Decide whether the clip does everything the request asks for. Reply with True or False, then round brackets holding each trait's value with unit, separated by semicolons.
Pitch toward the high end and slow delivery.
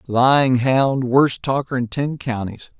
False (130 Hz; 130 wpm)